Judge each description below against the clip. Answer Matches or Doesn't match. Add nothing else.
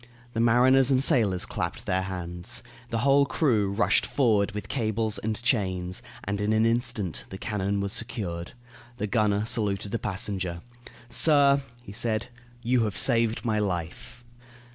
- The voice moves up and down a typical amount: Matches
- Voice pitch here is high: Doesn't match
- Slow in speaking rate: Doesn't match